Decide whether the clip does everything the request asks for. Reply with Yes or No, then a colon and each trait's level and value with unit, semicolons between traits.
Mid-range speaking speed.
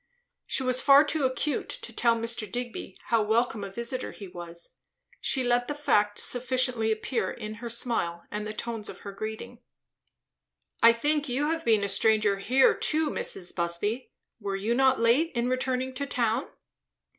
Yes: average, 170 wpm